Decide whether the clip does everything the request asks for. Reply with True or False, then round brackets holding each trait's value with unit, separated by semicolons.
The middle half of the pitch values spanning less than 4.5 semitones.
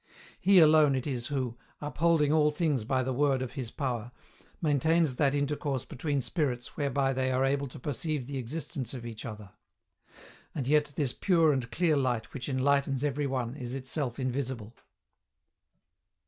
True (2.8 semitones)